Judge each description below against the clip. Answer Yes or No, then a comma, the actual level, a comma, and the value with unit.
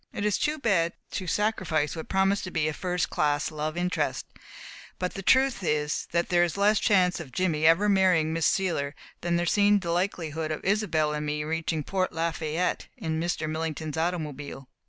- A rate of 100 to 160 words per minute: No, average, 190 wpm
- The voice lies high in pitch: No, medium, 170 Hz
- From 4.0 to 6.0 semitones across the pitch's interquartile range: No, average, 3.3 semitones